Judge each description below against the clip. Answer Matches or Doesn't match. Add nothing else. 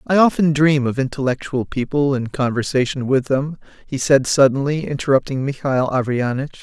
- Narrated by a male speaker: Matches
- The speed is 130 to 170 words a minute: Matches